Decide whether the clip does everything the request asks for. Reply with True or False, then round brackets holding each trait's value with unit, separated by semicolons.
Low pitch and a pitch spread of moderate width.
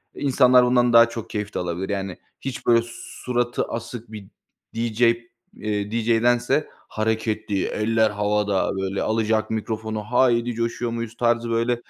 False (115 Hz; 1.9 semitones)